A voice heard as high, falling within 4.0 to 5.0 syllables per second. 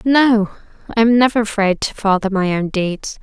Yes: high, 210 Hz; 4.9 syllables/s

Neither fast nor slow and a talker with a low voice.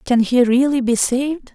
No: average, 195 wpm; very high, 255 Hz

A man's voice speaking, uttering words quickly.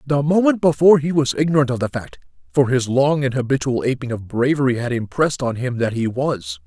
Yes: male; fast, 215 wpm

